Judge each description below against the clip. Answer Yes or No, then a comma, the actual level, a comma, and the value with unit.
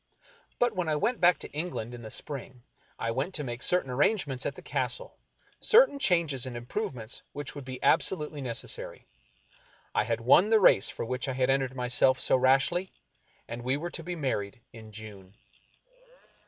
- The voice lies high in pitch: No, low, 135 Hz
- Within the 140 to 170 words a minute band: No, average, 185 wpm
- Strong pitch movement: Yes, wide, 6.1 semitones